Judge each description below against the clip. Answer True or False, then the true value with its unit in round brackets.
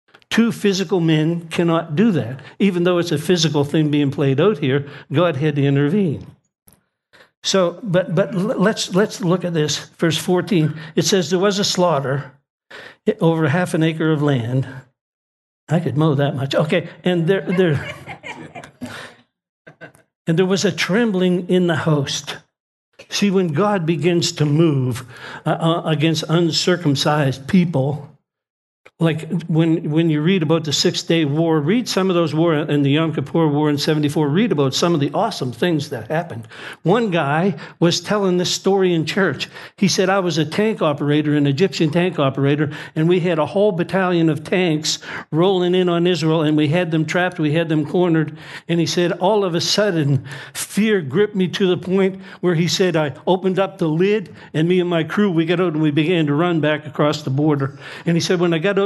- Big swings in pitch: False (3.3 semitones)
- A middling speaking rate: True (190 wpm)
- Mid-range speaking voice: True (165 Hz)